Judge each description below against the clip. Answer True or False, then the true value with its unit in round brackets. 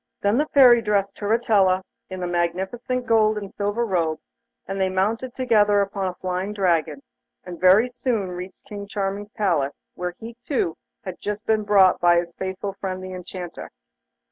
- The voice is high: True (195 Hz)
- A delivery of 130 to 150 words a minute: False (170 wpm)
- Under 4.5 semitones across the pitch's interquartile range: True (2.7 semitones)